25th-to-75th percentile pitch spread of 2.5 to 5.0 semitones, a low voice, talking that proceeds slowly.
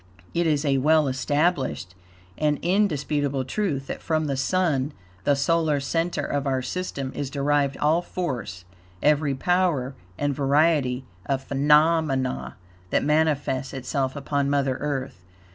No: average, 2.8 semitones; medium, 145 Hz; slow, 130 wpm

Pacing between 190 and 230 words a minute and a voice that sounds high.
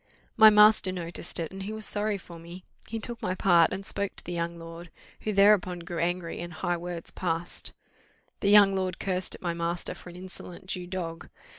No: fast, 205 wpm; medium, 180 Hz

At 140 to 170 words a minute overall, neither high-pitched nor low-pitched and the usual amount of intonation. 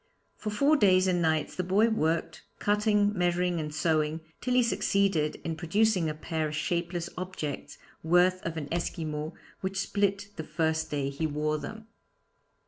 Yes: average, 160 wpm; medium, 170 Hz; average, 4.0 semitones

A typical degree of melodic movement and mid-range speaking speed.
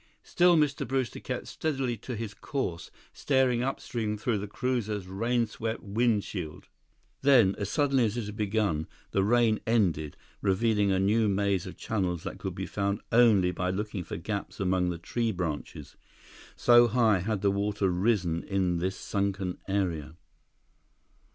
Yes: average, 3.8 semitones; average, 150 wpm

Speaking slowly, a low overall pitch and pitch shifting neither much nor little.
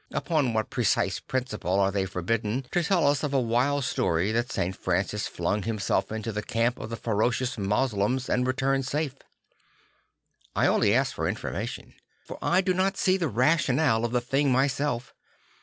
No: average, 175 wpm; low, 125 Hz; average, 4.4 semitones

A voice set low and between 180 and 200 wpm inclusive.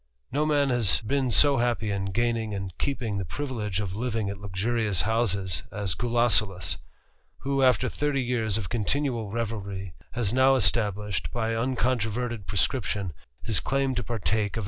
No: low, 115 Hz; average, 150 wpm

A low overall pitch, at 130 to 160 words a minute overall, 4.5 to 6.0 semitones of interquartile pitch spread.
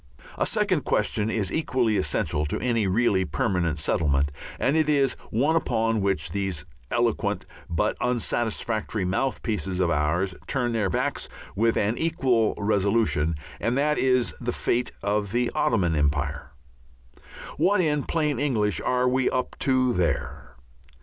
Yes: low, 115 Hz; average, 140 wpm; average, 5.2 semitones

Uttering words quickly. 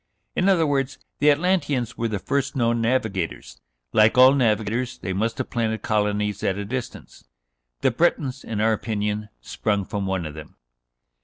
No: average, 165 wpm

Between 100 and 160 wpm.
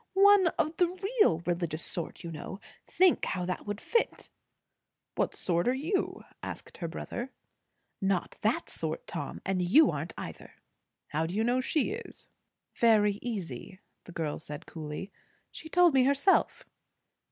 Yes: average, 150 wpm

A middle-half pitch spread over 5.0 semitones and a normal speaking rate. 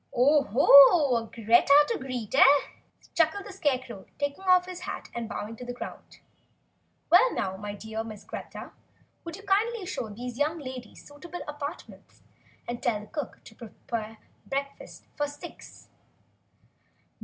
Yes: wide, 5.4 semitones; average, 150 wpm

